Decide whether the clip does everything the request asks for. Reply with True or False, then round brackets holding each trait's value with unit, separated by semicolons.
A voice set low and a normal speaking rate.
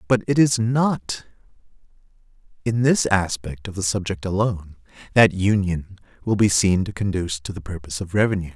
True (100 Hz; 160 wpm)